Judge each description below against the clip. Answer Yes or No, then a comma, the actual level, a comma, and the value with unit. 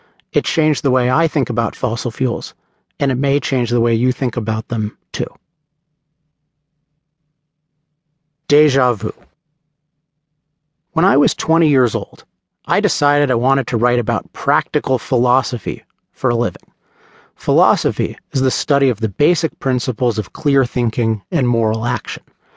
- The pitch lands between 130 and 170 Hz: Yes, medium, 140 Hz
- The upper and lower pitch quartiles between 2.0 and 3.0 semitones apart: No, average, 3.8 semitones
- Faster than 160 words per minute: No, average, 145 wpm